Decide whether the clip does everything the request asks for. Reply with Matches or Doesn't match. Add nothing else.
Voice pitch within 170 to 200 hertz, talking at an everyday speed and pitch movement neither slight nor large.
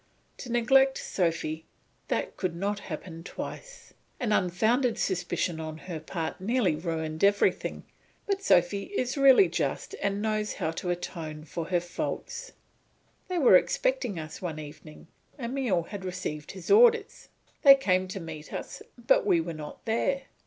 Doesn't match